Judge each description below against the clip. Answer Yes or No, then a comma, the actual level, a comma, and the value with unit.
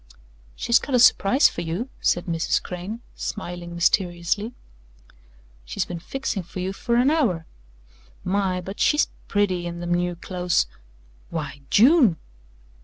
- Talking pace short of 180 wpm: Yes, slow, 135 wpm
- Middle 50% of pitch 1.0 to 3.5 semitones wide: No, average, 4.4 semitones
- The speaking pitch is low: No, medium, 180 Hz